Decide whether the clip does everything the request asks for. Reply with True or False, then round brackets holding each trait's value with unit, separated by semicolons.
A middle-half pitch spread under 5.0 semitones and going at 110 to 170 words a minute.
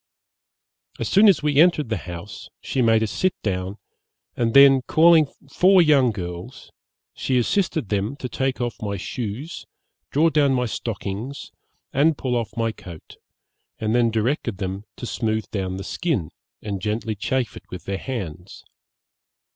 False (5.6 semitones; 155 wpm)